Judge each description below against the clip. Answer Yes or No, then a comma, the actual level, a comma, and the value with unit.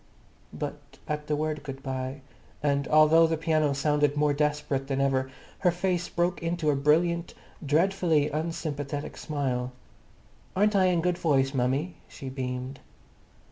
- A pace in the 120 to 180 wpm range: Yes, average, 140 wpm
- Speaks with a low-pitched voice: No, medium, 150 Hz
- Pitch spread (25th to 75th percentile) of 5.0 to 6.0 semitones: No, average, 3.3 semitones